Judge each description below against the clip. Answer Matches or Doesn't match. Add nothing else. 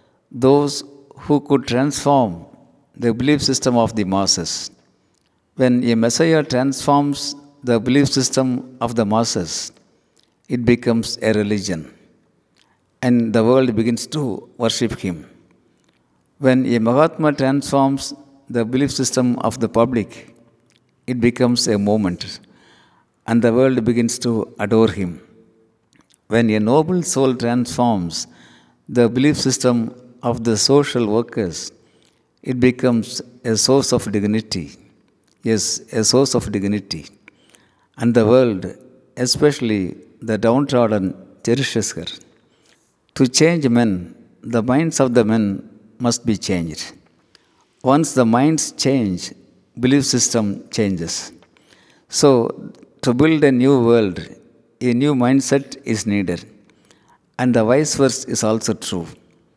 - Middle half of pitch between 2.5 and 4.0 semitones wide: Matches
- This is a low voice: Matches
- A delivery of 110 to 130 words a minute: Matches